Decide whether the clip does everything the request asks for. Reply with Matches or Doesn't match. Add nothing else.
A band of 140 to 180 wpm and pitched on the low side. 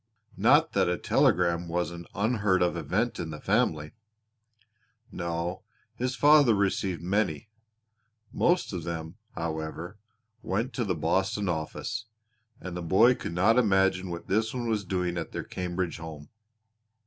Matches